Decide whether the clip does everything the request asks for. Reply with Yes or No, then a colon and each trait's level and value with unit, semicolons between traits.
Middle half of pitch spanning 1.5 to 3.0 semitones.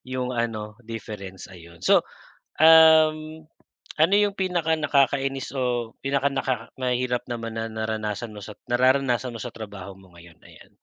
No: average, 4.4 semitones